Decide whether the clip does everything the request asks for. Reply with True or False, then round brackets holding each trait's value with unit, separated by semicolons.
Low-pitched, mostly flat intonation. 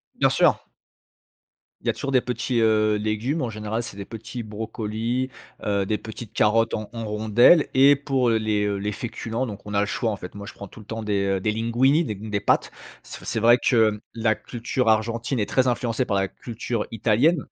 True (110 Hz; 2.3 semitones)